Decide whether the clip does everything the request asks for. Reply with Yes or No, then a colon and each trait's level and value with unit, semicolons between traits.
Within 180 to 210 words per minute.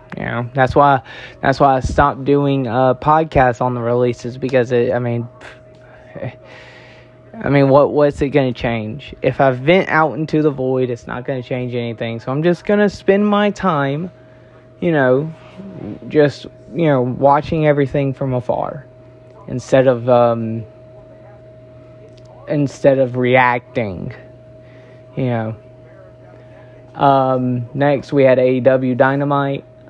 No: average, 140 wpm